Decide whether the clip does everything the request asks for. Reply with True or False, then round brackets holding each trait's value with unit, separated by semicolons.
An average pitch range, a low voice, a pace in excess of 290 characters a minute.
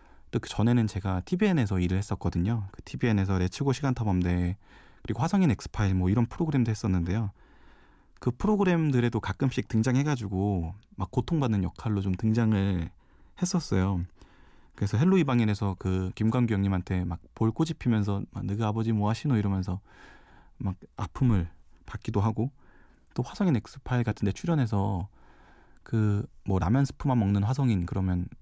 True (4.6 semitones; 105 Hz; 350 characters per minute)